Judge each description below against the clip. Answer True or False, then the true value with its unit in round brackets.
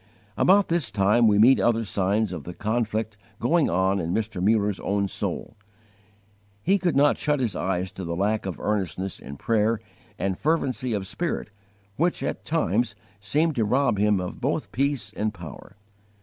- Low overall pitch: True (105 Hz)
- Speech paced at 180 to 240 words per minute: False (170 wpm)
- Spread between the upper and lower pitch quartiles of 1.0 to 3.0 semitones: False (4.8 semitones)